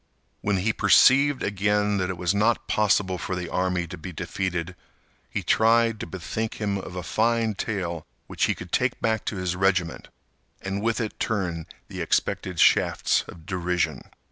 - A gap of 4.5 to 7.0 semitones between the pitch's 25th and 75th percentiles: No, average, 3.2 semitones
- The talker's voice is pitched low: Yes, very low, 95 Hz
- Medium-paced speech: Yes, average, 170 wpm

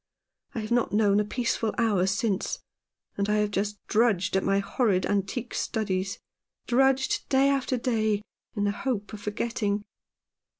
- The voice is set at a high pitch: Yes, high, 210 Hz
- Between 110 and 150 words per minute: No, average, 160 wpm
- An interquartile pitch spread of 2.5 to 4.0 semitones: Yes, average, 2.9 semitones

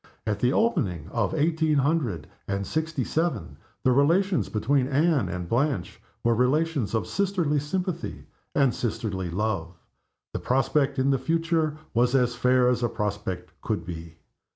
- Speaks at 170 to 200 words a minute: No, average, 150 wpm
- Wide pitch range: Yes, wide, 7.0 semitones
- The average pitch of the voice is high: No, low, 130 Hz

